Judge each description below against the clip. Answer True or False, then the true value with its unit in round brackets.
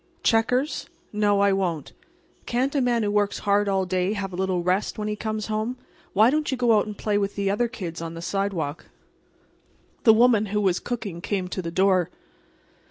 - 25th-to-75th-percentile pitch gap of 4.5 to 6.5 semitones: False (2.8 semitones)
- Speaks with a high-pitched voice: True (205 Hz)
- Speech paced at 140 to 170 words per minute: False (200 wpm)